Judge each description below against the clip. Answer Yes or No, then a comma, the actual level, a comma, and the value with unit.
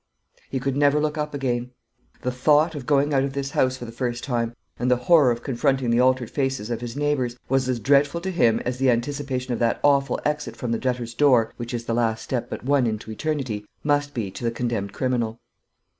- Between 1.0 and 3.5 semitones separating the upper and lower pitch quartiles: Yes, average, 3.1 semitones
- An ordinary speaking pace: No, fast, 225 wpm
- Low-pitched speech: Yes, low, 125 Hz